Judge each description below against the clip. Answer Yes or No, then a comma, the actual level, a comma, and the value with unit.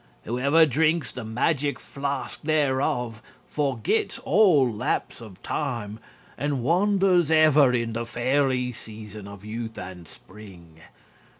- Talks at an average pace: No, slow, 115 wpm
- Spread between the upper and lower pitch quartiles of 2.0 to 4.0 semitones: No, average, 5.0 semitones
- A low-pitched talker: Yes, low, 125 Hz